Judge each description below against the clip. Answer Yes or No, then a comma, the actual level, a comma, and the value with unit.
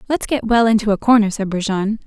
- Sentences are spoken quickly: Yes, fast, 230 wpm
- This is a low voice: No, high, 215 Hz